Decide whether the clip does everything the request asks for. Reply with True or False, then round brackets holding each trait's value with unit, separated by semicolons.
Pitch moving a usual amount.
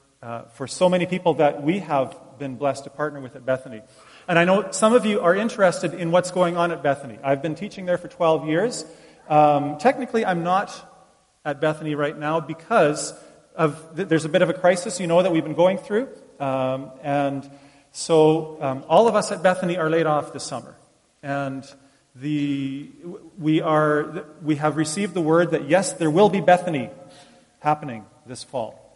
True (4.1 semitones)